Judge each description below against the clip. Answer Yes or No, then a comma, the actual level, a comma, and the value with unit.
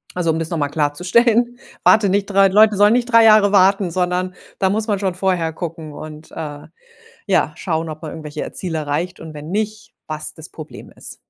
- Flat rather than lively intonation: No, average, 4.4 semitones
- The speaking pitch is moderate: Yes, medium, 180 Hz